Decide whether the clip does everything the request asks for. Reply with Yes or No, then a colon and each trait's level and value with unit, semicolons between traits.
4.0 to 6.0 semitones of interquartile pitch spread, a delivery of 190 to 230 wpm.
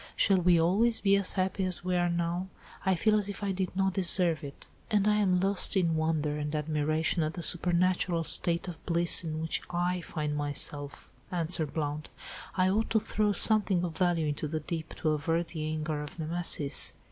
No: average, 3.0 semitones; average, 195 wpm